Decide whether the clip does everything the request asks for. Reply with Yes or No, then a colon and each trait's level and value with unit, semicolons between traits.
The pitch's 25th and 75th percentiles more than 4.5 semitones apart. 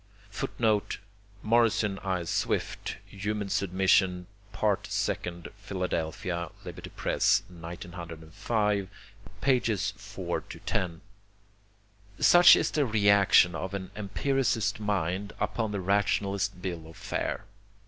No: average, 2.8 semitones